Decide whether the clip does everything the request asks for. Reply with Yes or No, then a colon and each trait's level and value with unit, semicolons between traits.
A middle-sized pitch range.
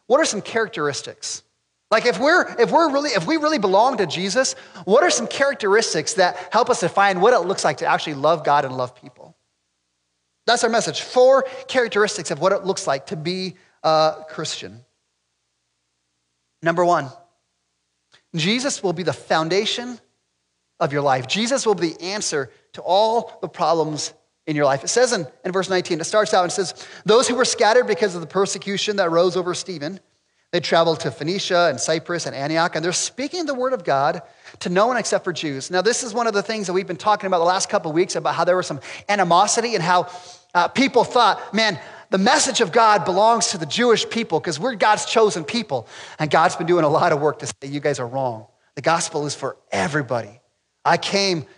No: wide, 5.9 semitones